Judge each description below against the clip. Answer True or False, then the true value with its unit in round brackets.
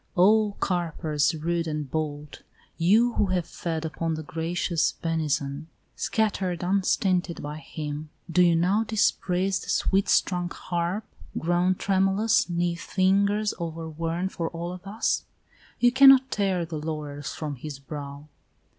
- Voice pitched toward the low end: False (175 Hz)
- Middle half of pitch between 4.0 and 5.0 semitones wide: False (3.5 semitones)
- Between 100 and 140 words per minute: True (135 wpm)